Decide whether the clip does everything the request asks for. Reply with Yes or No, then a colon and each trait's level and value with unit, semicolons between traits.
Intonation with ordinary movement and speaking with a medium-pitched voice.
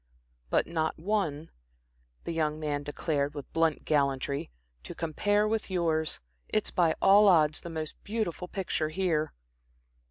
Yes: average, 3.6 semitones; medium, 160 Hz